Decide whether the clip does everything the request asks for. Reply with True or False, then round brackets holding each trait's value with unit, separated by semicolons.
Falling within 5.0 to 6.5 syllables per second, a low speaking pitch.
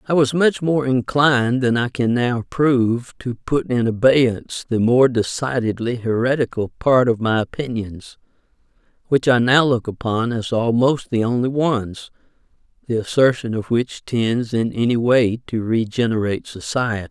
False (4.6 syllables/s; 120 Hz)